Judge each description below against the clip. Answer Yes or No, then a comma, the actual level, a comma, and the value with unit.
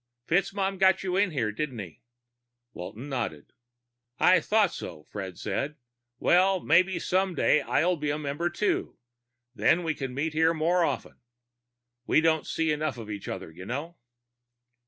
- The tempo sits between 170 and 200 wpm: No, average, 155 wpm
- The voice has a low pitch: No, medium, 155 Hz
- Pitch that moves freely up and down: Yes, wide, 6.2 semitones